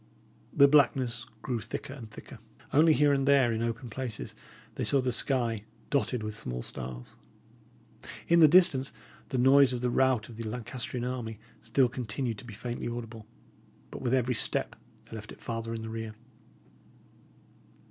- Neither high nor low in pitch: No, low, 120 Hz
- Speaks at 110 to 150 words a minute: No, average, 170 wpm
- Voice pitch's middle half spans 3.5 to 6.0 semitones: No, average, 2.8 semitones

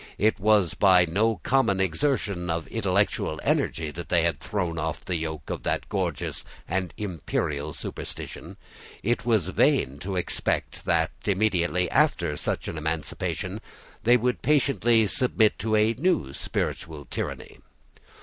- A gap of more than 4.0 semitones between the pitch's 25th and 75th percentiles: Yes, average, 5.0 semitones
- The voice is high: No, very low, 95 Hz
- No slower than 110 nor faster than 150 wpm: Yes, average, 140 wpm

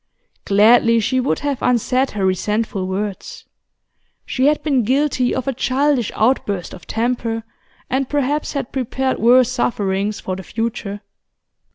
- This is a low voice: No, high, 240 Hz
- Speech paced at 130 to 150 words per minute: Yes, average, 140 wpm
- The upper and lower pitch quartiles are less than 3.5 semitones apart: No, average, 4.0 semitones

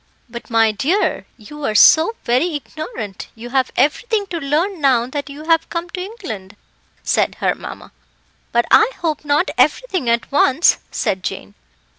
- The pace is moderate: Yes, average, 160 wpm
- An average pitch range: No, wide, 6.3 semitones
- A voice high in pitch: Yes, very high, 290 Hz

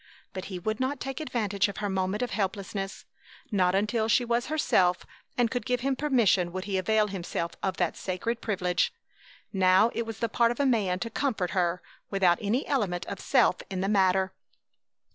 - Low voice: No, high, 205 Hz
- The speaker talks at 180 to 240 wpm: Yes, average, 190 wpm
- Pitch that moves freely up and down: No, average, 4.1 semitones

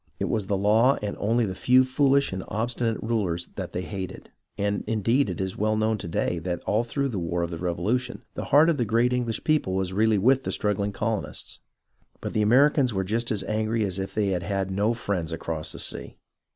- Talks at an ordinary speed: No, fast, 220 wpm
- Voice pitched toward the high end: No, low, 105 Hz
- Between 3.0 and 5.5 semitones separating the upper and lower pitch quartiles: Yes, average, 3.9 semitones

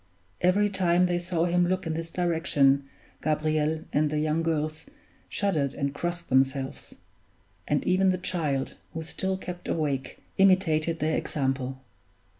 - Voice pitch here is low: No, medium, 160 Hz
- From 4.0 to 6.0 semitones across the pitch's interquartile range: No, average, 3.2 semitones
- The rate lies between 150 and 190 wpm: No, average, 140 wpm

